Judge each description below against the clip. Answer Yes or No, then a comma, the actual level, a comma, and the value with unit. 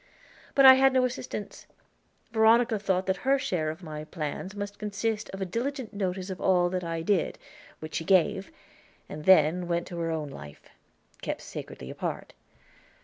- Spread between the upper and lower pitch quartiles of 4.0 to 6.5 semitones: Yes, average, 4.8 semitones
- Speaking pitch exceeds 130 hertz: Yes, high, 190 Hz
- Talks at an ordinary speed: Yes, average, 170 wpm